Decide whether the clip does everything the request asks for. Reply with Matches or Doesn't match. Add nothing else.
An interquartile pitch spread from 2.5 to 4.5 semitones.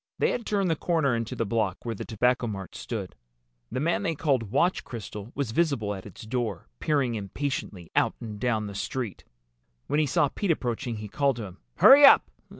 Doesn't match